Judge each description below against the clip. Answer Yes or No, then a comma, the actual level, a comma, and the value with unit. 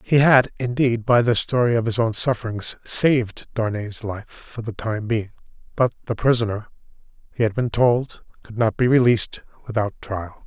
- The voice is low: Yes, low, 115 Hz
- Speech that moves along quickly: No, average, 170 wpm